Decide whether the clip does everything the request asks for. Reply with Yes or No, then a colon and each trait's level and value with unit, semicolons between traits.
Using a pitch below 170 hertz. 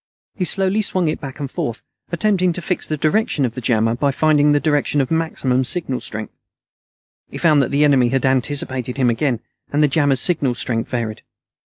Yes: medium, 140 Hz